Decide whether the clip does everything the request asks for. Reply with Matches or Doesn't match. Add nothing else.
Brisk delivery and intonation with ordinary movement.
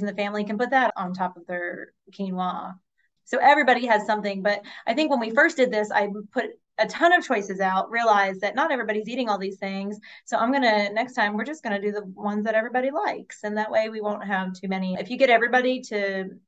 Matches